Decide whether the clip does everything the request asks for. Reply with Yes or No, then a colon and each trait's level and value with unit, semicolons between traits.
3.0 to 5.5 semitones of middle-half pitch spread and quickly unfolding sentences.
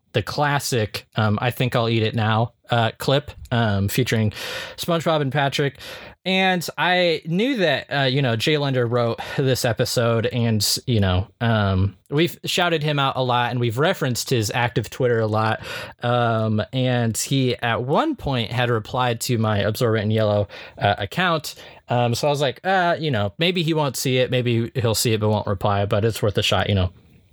No: average, 4.2 semitones; average, 195 wpm